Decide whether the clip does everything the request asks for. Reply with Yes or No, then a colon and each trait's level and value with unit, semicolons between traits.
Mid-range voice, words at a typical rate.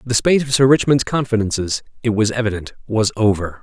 No: low, 115 Hz; average, 180 wpm